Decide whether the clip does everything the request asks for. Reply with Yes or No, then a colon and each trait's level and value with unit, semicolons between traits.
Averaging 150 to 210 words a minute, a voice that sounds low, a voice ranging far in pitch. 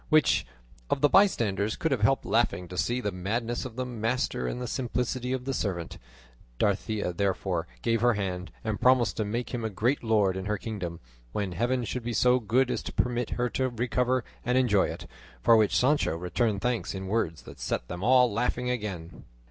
No: average, 200 wpm; low, 115 Hz; average, 3.9 semitones